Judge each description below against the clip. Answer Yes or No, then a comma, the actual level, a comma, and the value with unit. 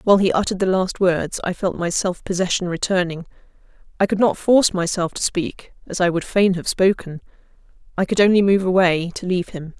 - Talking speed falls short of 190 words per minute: No, average, 195 wpm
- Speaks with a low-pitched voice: No, medium, 185 Hz